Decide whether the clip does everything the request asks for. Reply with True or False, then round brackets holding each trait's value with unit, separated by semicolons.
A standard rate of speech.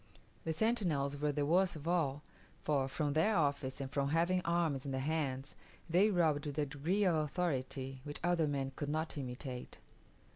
True (180 wpm)